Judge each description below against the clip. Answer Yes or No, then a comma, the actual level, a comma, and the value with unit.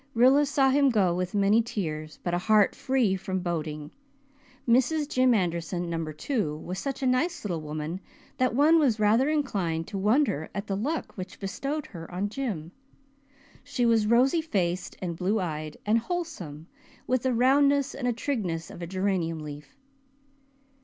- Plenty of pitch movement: Yes, wide, 7.2 semitones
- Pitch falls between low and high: No, high, 205 Hz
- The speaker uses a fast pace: No, average, 165 wpm